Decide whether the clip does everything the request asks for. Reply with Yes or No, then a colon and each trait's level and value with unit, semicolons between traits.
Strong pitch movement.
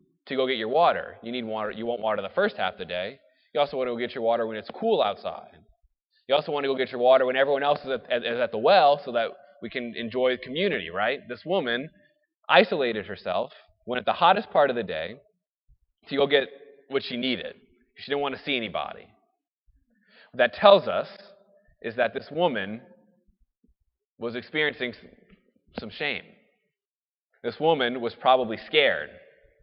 Yes: wide, 8.4 semitones